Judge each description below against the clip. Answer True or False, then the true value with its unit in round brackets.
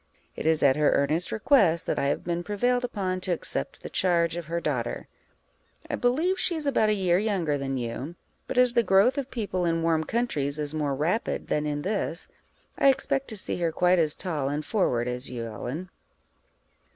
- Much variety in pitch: True (6.5 semitones)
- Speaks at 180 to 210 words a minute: True (200 wpm)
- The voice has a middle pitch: True (170 Hz)